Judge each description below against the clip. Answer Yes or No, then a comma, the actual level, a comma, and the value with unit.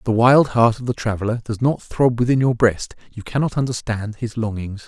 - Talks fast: Yes, fast, 210 wpm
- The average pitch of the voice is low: Yes, low, 115 Hz